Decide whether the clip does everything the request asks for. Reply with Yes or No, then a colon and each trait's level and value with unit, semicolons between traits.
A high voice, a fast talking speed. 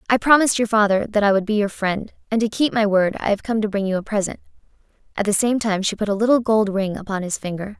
Yes: high, 210 Hz; fast, 275 wpm